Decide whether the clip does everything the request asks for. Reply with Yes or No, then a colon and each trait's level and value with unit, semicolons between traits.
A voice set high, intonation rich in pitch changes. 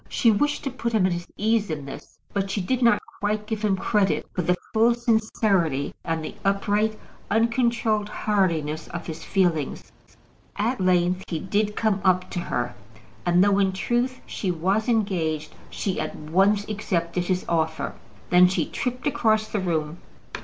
No: high, 195 Hz; average, 3.9 semitones